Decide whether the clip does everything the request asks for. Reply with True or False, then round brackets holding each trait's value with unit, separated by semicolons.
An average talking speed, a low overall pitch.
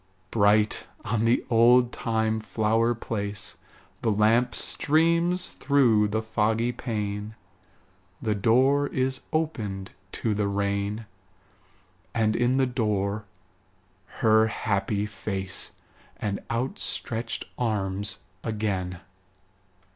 False (95 wpm; 110 Hz)